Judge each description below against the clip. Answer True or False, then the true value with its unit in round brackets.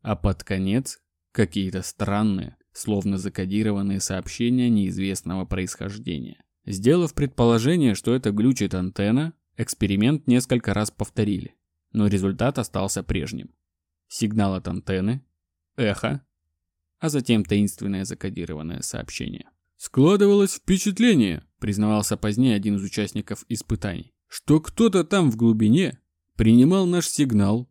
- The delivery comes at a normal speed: False (105 wpm)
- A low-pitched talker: True (105 Hz)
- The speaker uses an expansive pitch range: False (4.4 semitones)